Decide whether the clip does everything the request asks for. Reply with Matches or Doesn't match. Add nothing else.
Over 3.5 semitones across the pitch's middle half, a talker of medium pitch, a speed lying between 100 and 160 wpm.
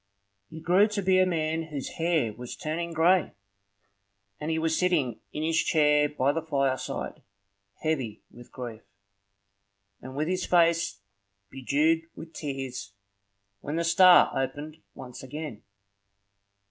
Matches